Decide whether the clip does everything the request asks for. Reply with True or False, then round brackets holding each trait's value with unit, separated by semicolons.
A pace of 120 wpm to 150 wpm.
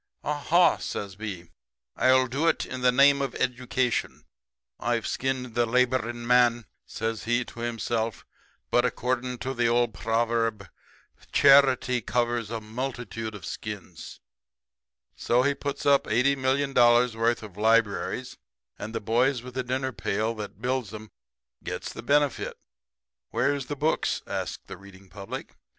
True (145 wpm)